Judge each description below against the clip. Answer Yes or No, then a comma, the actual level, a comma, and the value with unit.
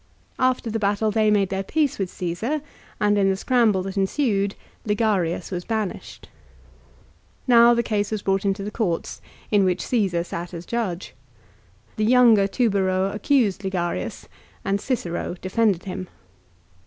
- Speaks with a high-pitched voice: Yes, high, 200 Hz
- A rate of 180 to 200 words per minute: No, average, 145 wpm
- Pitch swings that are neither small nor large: Yes, average, 3.1 semitones